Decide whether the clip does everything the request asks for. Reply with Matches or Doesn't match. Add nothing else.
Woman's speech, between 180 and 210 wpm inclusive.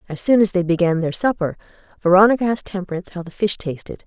Matches